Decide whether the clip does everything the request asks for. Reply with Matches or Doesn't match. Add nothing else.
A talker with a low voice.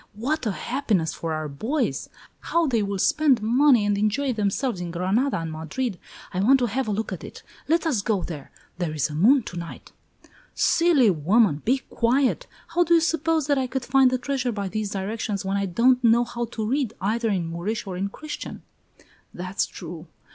Doesn't match